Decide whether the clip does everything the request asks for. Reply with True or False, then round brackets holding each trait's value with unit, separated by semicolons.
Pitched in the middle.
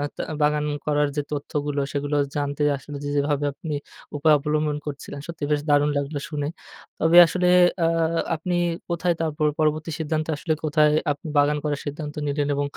True (150 Hz)